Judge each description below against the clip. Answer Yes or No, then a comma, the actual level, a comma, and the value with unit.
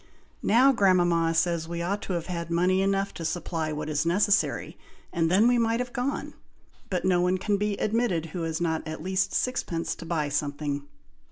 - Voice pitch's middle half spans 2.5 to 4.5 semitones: Yes, average, 3.4 semitones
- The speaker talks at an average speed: Yes, average, 190 wpm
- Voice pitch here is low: No, medium, 175 Hz